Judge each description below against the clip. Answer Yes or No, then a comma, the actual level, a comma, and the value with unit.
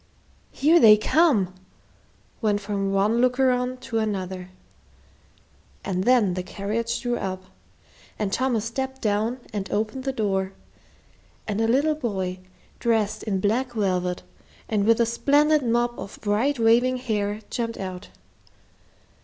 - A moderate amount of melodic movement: Yes, average, 3.9 semitones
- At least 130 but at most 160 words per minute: Yes, slow, 135 wpm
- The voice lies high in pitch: Yes, high, 220 Hz